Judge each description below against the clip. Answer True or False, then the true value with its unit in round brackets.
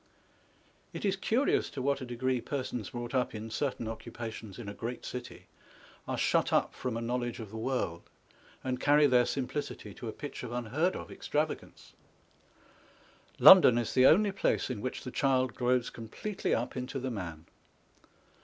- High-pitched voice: False (125 Hz)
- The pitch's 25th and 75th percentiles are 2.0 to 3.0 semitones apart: True (2.7 semitones)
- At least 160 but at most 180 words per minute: True (170 wpm)